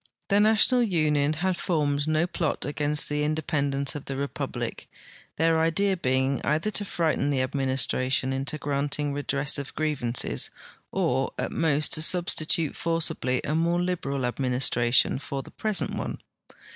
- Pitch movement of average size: Yes, average, 3.1 semitones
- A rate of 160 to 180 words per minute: No, average, 150 wpm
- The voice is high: No, medium, 150 Hz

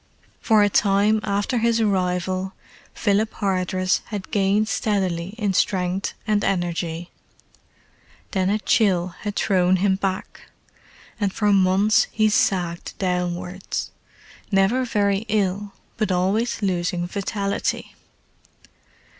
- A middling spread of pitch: No, narrow, 2.2 semitones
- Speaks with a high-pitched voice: Yes, high, 195 Hz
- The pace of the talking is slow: Yes, slow, 110 wpm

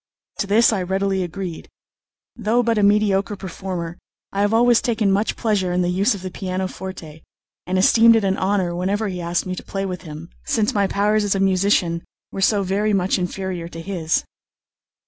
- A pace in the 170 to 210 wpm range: Yes, average, 190 wpm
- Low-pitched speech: No, high, 195 Hz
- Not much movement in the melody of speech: Yes, narrow, 2.3 semitones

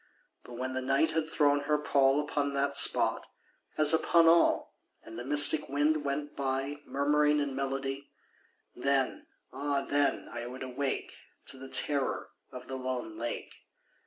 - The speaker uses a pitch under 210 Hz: Yes, medium, 140 Hz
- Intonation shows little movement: Yes, narrow, 1.8 semitones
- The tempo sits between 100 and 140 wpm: No, average, 150 wpm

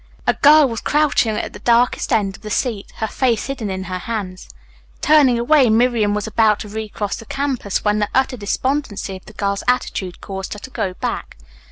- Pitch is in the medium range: No, high, 220 Hz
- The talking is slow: No, average, 200 wpm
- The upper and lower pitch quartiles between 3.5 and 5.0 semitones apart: Yes, average, 3.8 semitones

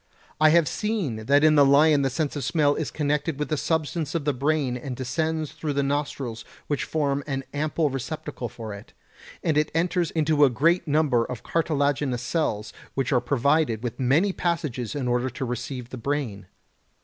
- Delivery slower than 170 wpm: No, average, 185 wpm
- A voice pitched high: No, medium, 145 Hz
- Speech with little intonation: No, average, 3.7 semitones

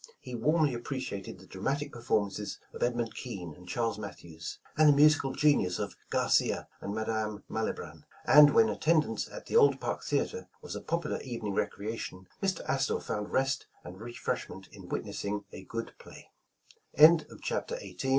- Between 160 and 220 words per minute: No, average, 150 wpm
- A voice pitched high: No, low, 115 Hz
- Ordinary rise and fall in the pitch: No, wide, 6.0 semitones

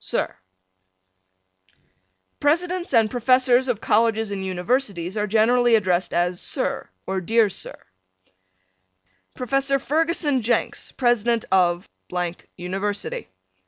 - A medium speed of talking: No, slow, 95 wpm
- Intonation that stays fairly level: No, average, 4.9 semitones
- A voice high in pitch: Yes, high, 225 Hz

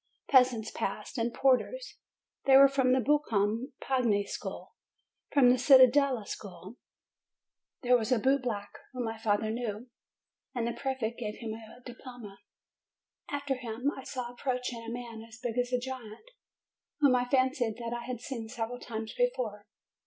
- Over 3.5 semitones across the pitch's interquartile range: No, average, 2.7 semitones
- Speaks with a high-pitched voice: Yes, high, 245 Hz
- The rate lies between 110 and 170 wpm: Yes, average, 155 wpm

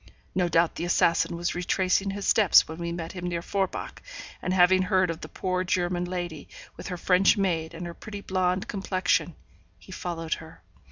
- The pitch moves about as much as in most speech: No, narrow, 1.7 semitones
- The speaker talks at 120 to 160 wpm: No, average, 185 wpm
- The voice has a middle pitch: Yes, medium, 180 Hz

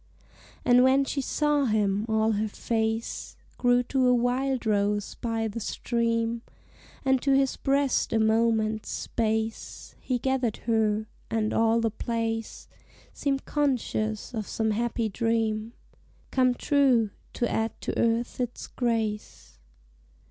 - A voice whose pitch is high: Yes, high, 230 Hz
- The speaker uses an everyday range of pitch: No, narrow, 2.3 semitones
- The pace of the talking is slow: Yes, slow, 125 wpm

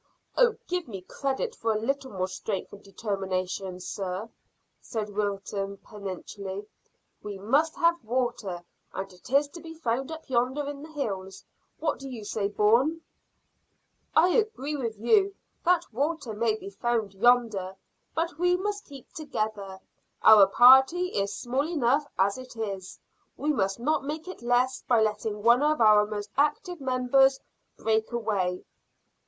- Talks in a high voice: Yes, high, 235 Hz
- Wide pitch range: Yes, wide, 6.2 semitones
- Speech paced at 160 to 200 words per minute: No, average, 150 wpm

